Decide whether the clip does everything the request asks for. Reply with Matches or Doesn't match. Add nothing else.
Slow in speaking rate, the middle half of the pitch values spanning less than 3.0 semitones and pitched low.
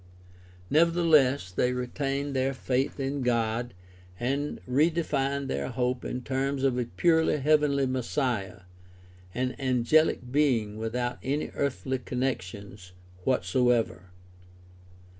Matches